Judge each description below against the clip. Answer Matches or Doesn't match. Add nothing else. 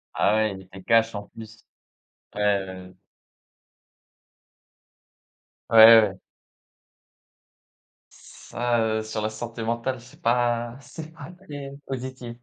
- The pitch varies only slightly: Matches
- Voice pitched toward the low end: Matches